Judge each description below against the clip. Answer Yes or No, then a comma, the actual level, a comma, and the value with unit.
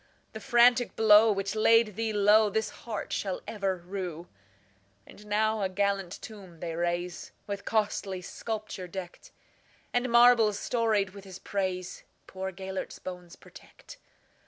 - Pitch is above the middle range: Yes, high, 200 Hz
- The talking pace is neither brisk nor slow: No, slow, 115 wpm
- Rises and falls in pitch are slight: No, average, 3.1 semitones